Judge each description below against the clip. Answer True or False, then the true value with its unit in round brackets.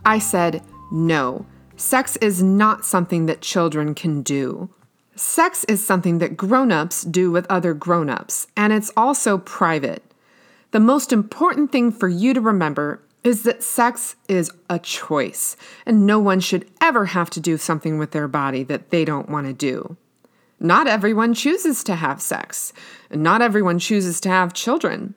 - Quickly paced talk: False (165 wpm)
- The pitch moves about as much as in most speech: False (5.7 semitones)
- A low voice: False (190 Hz)